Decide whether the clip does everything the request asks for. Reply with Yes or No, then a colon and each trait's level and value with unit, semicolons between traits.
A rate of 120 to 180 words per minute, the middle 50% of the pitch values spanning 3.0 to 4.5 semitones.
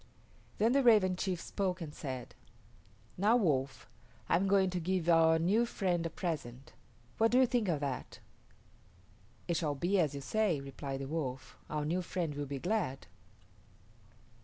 No: average, 165 wpm; average, 5.3 semitones